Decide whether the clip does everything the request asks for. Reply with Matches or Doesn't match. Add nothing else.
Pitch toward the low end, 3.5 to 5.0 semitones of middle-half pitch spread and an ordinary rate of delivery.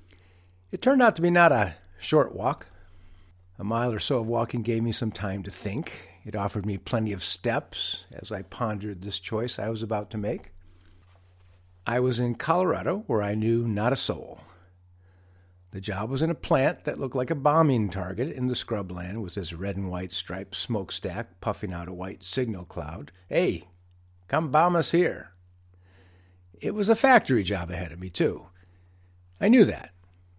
Matches